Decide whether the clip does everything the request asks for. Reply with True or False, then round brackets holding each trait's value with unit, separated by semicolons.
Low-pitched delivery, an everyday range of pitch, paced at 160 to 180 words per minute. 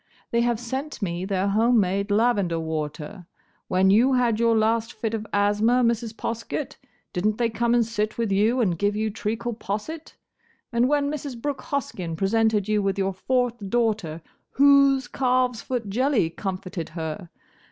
False (220 Hz; 3.6 semitones; 165 wpm)